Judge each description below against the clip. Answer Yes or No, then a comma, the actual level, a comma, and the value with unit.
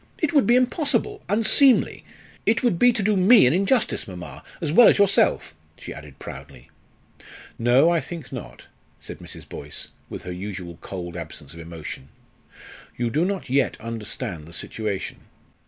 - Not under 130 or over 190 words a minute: Yes, average, 160 wpm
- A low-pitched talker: Yes, low, 130 Hz